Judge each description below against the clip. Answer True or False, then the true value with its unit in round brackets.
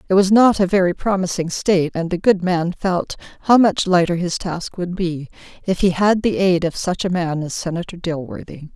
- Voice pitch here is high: False (180 Hz)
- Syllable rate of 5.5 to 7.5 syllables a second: False (5.1 syllables/s)